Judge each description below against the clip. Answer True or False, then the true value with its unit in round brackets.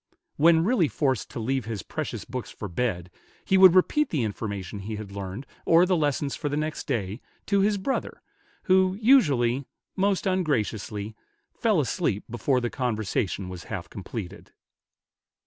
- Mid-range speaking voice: False (130 Hz)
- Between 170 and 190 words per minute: False (155 wpm)